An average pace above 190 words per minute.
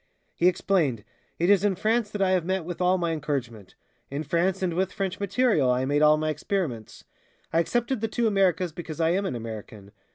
Yes: fast, 205 wpm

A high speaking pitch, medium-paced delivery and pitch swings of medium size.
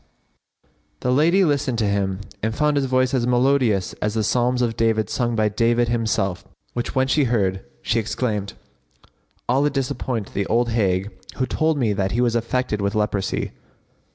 No: low, 115 Hz; average, 175 wpm; average, 3.5 semitones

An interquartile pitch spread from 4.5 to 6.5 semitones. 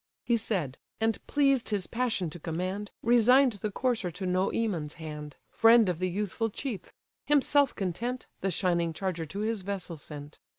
Yes: average, 4.9 semitones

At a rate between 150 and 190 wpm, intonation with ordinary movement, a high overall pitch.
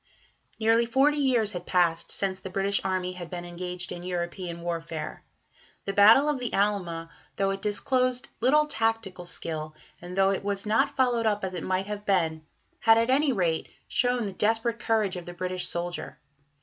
Yes: average, 180 wpm; average, 4.3 semitones; high, 195 Hz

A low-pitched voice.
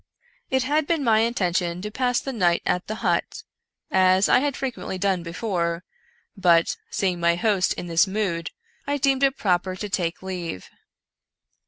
No: high, 190 Hz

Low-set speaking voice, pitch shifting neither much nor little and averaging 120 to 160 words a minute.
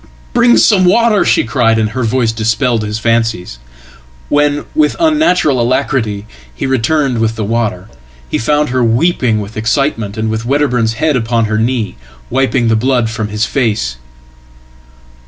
Yes: low, 115 Hz; average, 3.8 semitones; average, 140 wpm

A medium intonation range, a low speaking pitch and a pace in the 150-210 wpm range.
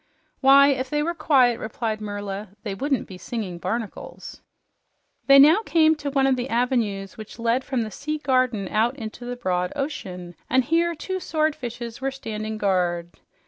No: average, 4.6 semitones; high, 245 Hz; average, 170 wpm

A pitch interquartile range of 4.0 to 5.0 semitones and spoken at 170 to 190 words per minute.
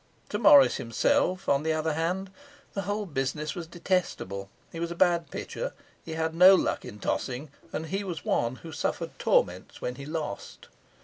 Yes: average, 4.6 semitones; average, 180 wpm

